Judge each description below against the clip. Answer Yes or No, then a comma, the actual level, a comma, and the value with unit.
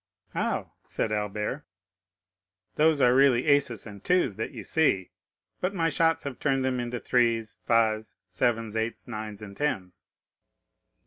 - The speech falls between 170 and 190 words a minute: No, average, 140 wpm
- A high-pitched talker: No, low, 120 Hz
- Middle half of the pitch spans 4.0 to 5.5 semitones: Yes, average, 4.6 semitones